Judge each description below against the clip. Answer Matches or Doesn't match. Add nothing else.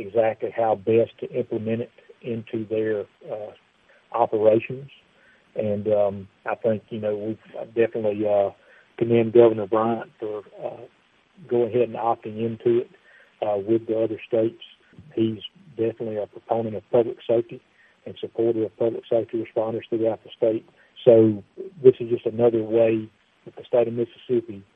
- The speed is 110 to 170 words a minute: Matches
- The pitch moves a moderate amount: Doesn't match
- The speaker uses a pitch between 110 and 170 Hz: Matches